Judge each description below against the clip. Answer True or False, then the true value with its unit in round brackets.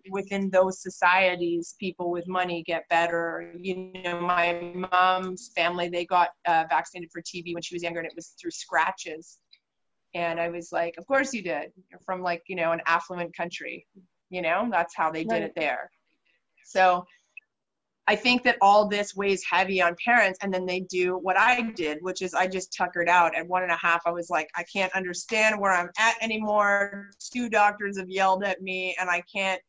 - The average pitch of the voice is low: False (185 Hz)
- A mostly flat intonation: True (2.2 semitones)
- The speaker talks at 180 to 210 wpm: True (200 wpm)